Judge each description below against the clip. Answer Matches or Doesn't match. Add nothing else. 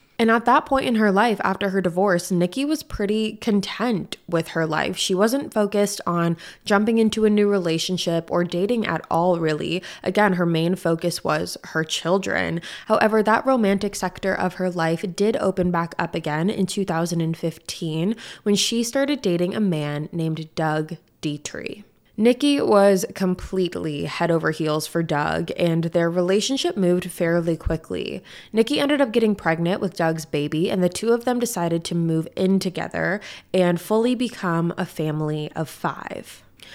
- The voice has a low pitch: Doesn't match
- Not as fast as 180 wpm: Matches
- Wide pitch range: Doesn't match